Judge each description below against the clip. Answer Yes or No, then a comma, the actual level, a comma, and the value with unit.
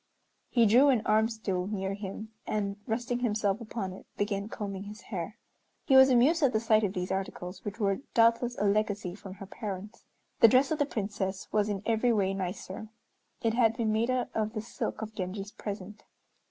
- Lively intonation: No, average, 2.7 semitones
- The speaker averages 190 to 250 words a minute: Yes, average, 195 wpm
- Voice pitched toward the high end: Yes, high, 215 Hz